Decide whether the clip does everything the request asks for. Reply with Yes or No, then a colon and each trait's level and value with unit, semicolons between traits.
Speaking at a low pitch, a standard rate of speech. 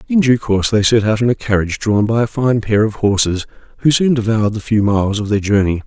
No: low, 110 Hz; fast, 255 wpm